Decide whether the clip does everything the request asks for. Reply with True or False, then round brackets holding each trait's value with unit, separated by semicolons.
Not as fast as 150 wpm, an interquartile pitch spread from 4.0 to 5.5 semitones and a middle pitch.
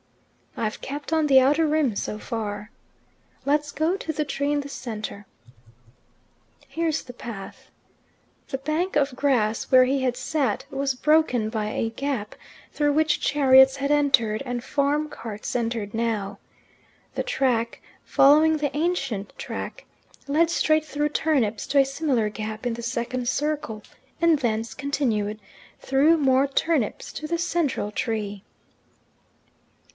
False (140 wpm; 4.7 semitones; 270 Hz)